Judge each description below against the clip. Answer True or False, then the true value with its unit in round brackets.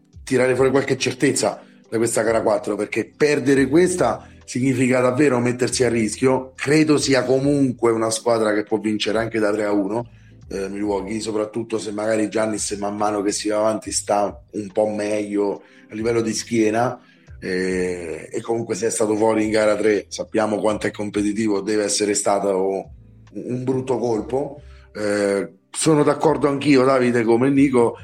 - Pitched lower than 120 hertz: True (110 Hz)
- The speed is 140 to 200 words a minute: True (165 wpm)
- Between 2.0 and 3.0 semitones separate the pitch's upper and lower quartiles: False (3.4 semitones)